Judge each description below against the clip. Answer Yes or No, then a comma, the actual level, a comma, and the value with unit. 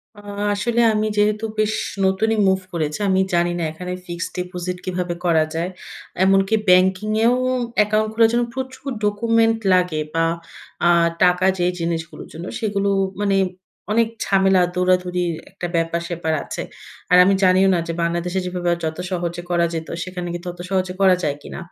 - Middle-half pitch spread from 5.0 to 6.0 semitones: No, average, 3.1 semitones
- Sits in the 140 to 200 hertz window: Yes, medium, 185 Hz